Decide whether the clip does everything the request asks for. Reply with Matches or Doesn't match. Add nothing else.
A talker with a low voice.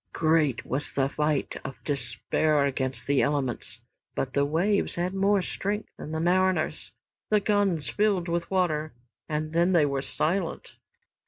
Doesn't match